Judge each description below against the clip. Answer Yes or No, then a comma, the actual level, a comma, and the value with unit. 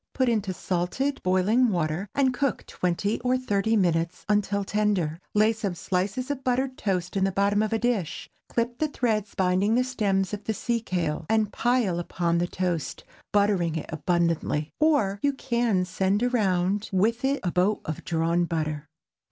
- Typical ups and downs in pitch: Yes, average, 4.7 semitones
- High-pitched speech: Yes, high, 200 Hz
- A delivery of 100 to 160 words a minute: No, average, 170 wpm